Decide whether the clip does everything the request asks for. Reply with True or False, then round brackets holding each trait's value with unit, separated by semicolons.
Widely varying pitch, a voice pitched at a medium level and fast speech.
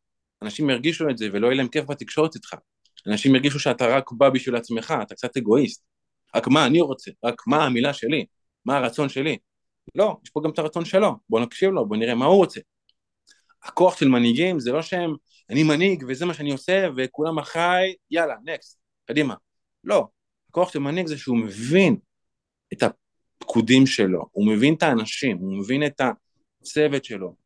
True (5.9 semitones; 145 Hz; 180 wpm)